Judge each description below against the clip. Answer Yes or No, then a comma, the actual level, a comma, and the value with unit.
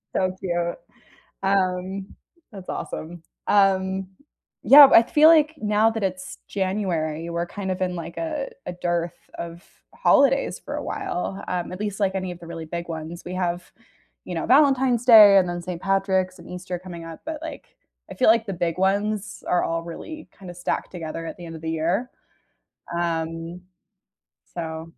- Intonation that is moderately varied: Yes, average, 3.1 semitones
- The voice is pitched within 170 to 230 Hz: Yes, medium, 185 Hz